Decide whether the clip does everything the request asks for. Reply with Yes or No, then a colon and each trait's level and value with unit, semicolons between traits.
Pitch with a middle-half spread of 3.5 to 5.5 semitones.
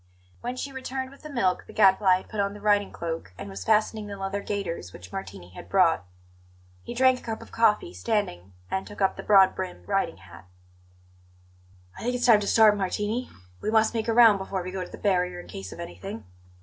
Yes: average, 3.8 semitones